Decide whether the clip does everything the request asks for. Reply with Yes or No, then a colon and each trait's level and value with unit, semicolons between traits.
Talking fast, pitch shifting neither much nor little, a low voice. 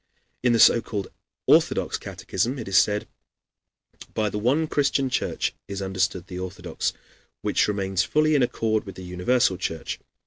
No: average, 160 wpm; average, 4.5 semitones; low, 105 Hz